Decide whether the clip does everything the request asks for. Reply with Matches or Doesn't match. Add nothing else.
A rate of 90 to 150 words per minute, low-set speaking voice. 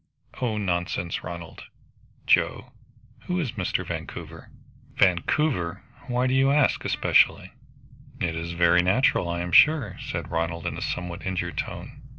Matches